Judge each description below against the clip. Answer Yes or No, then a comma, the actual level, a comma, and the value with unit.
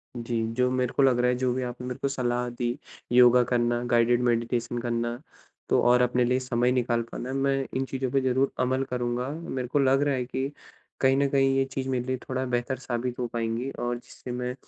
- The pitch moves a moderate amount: No, narrow, 1.4 semitones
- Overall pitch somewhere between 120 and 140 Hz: Yes, low, 125 Hz